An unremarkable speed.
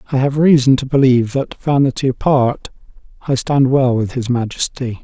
Yes: average, 165 wpm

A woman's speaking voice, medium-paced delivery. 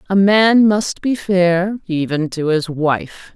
Yes: female; average, 160 wpm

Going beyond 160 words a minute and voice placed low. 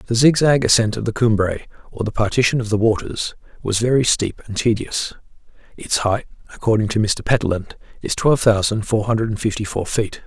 Yes: average, 180 wpm; low, 110 Hz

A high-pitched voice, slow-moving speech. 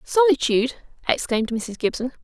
Yes: very high, 270 Hz; slow, 105 wpm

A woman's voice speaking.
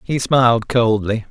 No: male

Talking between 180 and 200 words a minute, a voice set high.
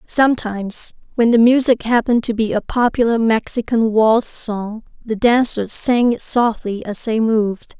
No: average, 155 wpm; high, 225 Hz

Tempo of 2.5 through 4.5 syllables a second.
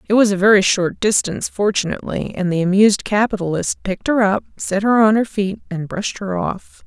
No: 5.7 syllables/s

